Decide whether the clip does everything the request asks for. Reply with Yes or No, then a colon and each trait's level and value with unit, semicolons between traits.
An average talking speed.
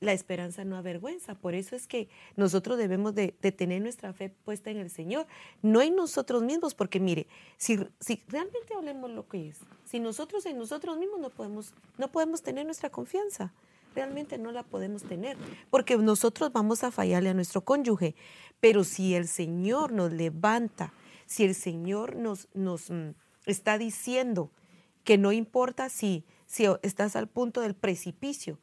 Yes: average, 170 wpm